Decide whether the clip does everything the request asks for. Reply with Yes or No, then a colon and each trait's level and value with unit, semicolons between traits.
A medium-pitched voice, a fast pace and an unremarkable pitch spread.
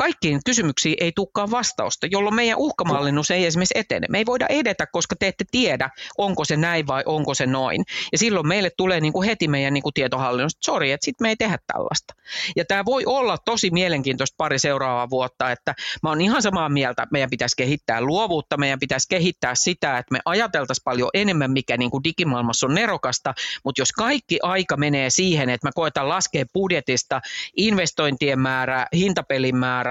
No: medium, 155 Hz; fast, 190 wpm; wide, 5.8 semitones